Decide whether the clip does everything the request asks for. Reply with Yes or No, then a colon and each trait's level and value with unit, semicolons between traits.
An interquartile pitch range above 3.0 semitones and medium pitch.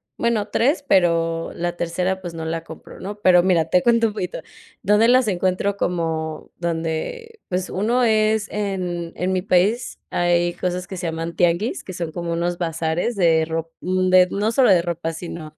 Yes: average, 3.4 semitones; medium, 180 Hz